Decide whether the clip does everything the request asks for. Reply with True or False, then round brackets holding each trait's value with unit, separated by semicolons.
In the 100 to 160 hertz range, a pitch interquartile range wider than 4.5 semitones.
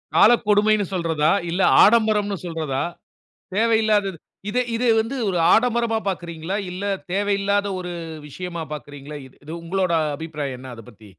False (185 Hz; 4.9 semitones)